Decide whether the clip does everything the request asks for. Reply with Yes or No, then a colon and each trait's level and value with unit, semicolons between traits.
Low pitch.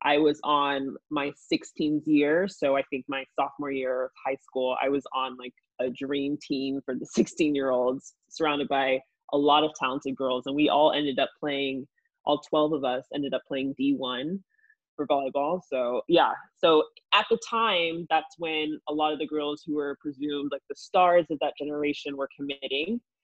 No: medium, 145 Hz